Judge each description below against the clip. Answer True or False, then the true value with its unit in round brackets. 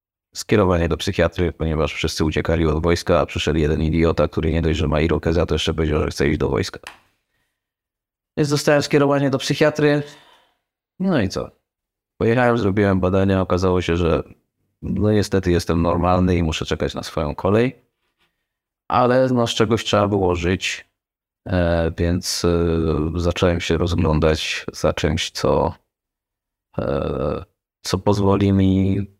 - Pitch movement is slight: False (3.8 semitones)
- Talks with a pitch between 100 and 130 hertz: False (90 Hz)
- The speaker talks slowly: False (140 wpm)